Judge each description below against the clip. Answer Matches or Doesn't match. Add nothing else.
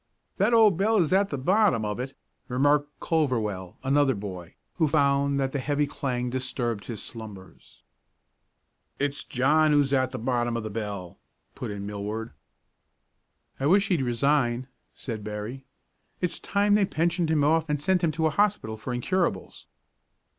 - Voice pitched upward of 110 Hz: Matches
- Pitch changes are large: Matches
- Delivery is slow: Doesn't match